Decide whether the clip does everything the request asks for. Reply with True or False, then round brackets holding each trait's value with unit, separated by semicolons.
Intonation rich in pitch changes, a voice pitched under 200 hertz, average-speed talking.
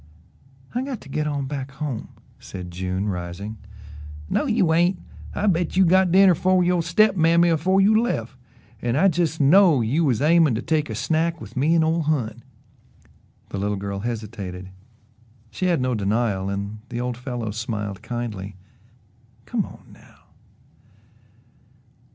True (7.9 semitones; 135 Hz; 155 wpm)